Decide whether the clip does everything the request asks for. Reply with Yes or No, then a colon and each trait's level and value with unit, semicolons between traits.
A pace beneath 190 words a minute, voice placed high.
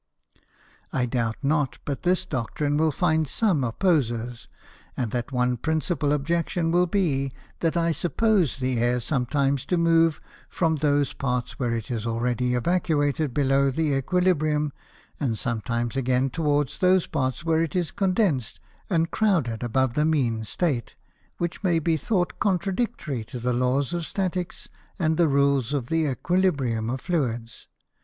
No: average, 150 wpm; medium, 145 Hz